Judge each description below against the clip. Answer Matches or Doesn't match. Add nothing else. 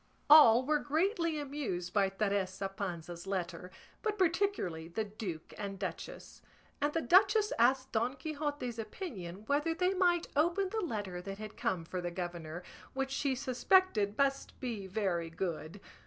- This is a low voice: Doesn't match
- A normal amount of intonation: Doesn't match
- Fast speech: Doesn't match